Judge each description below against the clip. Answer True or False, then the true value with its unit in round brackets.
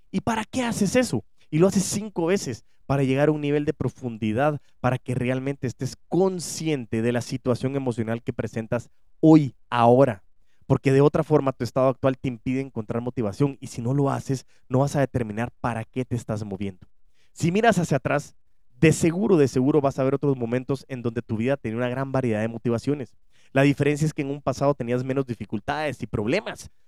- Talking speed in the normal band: False (200 wpm)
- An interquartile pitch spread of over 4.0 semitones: False (3.4 semitones)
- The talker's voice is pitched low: True (130 Hz)